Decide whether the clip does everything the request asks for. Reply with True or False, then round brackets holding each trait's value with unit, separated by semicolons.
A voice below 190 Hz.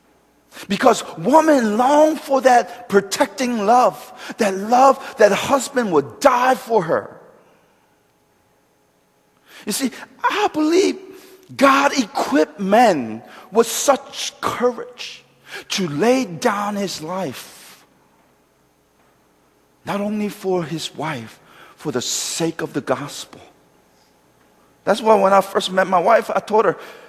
False (210 Hz)